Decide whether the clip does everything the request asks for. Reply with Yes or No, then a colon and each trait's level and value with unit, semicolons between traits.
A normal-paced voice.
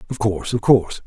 No: fast, 225 wpm